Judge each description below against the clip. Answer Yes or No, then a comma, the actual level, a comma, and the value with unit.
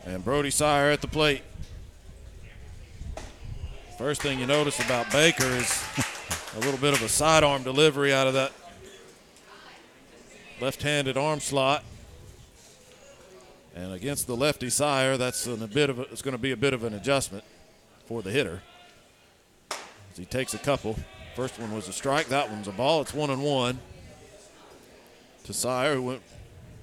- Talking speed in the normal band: Yes, average, 160 wpm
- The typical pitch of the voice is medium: No, low, 125 Hz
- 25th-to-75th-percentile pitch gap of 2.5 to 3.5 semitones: No, average, 5.1 semitones